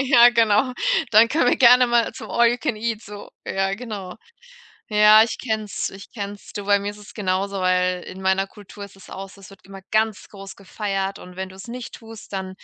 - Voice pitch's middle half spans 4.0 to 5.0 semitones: No, narrow, 2.6 semitones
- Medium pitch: No, high, 205 Hz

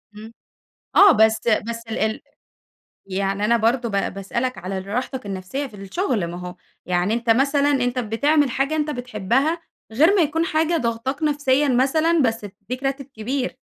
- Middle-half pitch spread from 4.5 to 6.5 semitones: Yes, average, 5.0 semitones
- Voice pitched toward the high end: Yes, high, 245 Hz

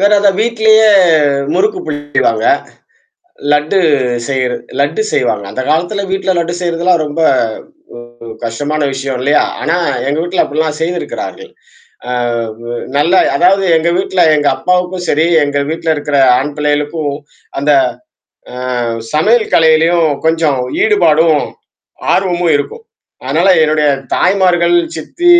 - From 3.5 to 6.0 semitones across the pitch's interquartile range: Yes, average, 3.8 semitones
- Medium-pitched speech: Yes, medium, 160 Hz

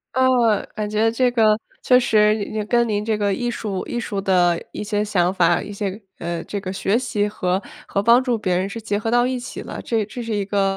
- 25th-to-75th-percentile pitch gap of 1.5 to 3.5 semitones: Yes, average, 2.7 semitones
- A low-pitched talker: No, high, 210 Hz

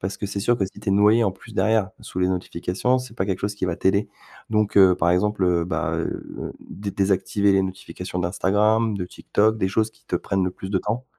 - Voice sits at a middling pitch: No, low, 100 Hz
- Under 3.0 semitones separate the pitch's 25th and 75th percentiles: Yes, narrow, 2.4 semitones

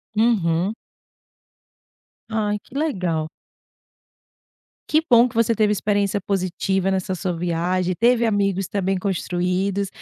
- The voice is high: Yes, high, 195 Hz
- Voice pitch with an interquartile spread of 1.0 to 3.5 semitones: Yes, average, 2.9 semitones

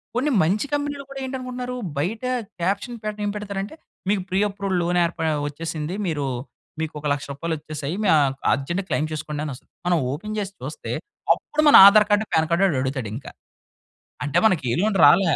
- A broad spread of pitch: Yes, wide, 5.8 semitones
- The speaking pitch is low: No, medium, 180 Hz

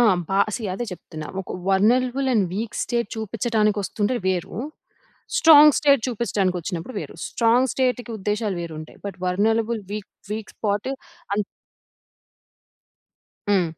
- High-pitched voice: Yes, high, 215 Hz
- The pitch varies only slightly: No, average, 3.8 semitones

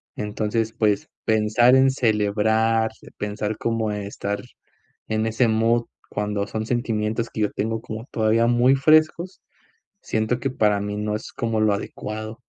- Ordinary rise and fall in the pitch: No, narrow, 1.7 semitones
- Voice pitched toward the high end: No, low, 110 Hz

